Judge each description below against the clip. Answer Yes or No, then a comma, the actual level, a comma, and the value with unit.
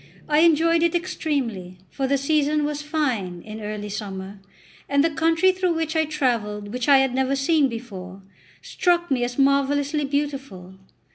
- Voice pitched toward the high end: Yes, very high, 275 Hz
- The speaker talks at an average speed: Yes, average, 165 wpm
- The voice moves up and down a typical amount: No, wide, 6.1 semitones